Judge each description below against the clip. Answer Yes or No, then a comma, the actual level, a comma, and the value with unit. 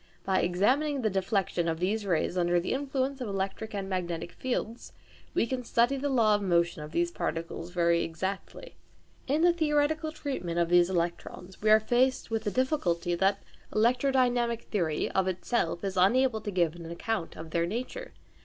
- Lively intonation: Yes, wide, 6.5 semitones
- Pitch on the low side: No, high, 200 Hz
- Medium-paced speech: Yes, average, 175 wpm